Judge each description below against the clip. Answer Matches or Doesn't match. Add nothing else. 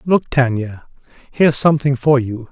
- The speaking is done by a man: Matches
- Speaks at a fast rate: Doesn't match